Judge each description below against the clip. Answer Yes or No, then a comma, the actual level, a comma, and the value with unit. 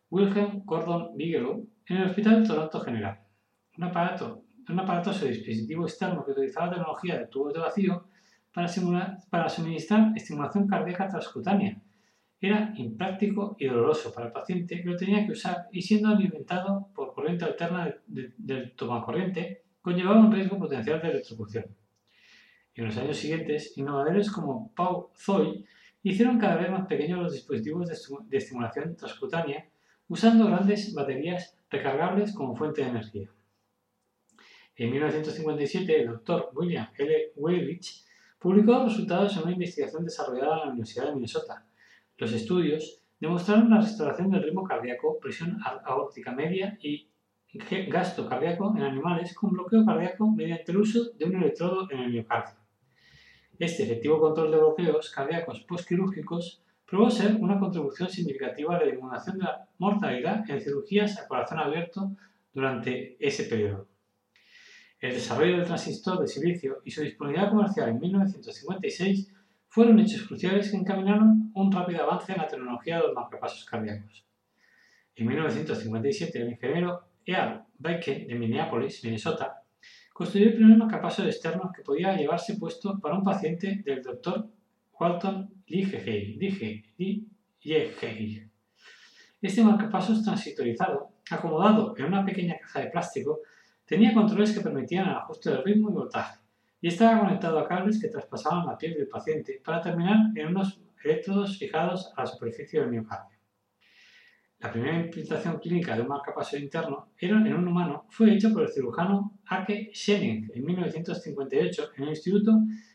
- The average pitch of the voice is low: No, medium, 180 Hz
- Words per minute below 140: No, average, 150 wpm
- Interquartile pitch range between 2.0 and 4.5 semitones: No, average, 5.1 semitones